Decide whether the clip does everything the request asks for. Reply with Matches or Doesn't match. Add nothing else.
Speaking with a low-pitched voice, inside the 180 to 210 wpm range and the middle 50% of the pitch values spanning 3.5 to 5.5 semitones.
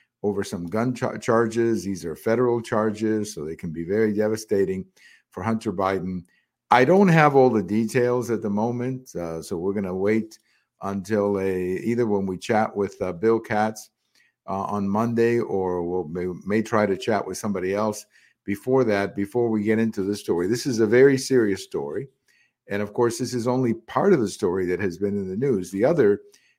Doesn't match